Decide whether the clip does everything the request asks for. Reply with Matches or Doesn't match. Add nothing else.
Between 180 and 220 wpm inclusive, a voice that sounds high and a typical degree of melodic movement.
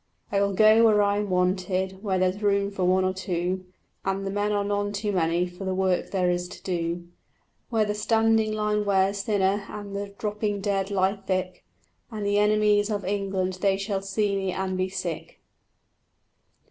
Doesn't match